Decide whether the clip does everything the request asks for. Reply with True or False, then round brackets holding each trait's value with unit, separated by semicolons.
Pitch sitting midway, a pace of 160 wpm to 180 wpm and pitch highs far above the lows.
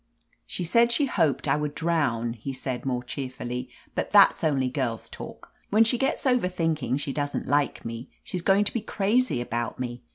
False (145 Hz; 190 wpm; 7.6 semitones)